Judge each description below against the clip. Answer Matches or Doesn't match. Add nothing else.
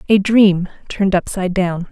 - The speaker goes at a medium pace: Matches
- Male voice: Doesn't match